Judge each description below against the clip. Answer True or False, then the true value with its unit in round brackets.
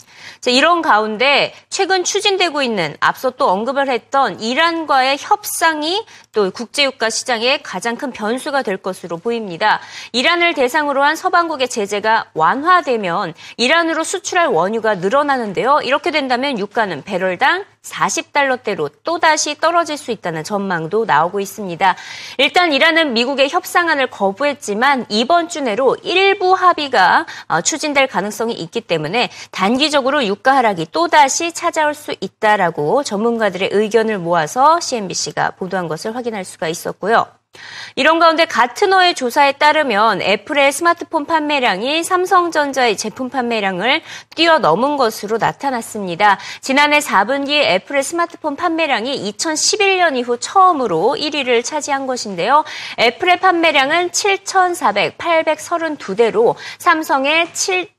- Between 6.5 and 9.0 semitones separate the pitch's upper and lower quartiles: True (6.8 semitones)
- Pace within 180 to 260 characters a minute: False (315 characters per minute)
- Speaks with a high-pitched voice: True (280 Hz)